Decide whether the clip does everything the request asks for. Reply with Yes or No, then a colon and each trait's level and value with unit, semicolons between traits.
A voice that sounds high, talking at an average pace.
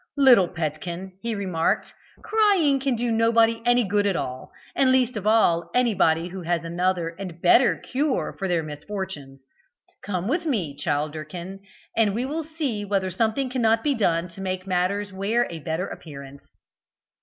Yes: high, 195 Hz; average, 160 wpm